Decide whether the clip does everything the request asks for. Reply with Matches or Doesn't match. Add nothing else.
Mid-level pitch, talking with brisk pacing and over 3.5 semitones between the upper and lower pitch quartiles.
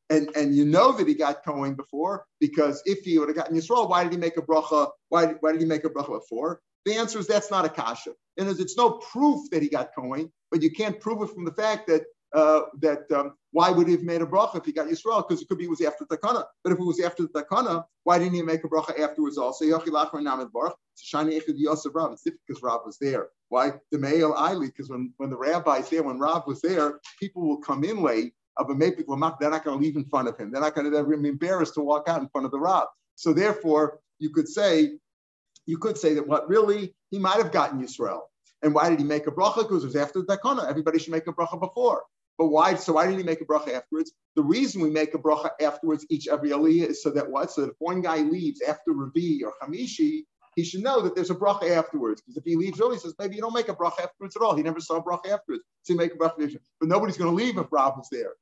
Matches